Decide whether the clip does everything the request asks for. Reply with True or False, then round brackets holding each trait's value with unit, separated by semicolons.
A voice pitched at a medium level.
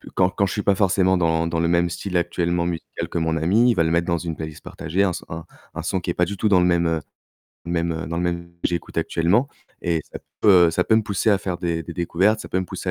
False (85 Hz)